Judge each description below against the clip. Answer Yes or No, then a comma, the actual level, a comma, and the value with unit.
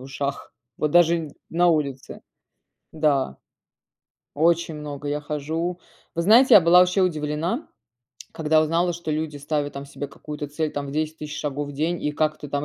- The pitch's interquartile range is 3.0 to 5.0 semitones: No, narrow, 2.5 semitones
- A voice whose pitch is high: No, medium, 155 Hz